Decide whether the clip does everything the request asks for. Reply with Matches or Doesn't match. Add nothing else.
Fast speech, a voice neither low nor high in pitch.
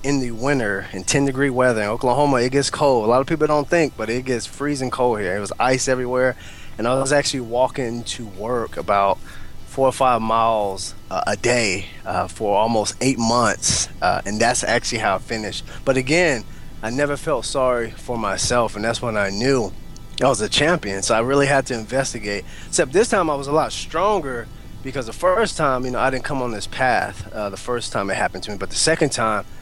Doesn't match